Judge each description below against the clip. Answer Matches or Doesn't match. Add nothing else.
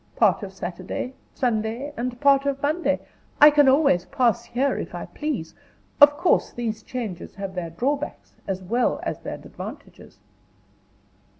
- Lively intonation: Matches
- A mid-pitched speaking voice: Doesn't match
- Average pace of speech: Matches